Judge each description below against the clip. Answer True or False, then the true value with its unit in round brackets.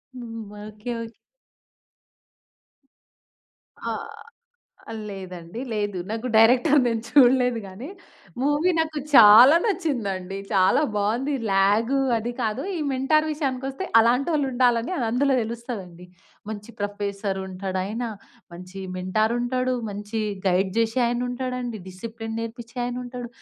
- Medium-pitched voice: False (230 Hz)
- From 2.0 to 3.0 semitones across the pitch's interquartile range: False (3.8 semitones)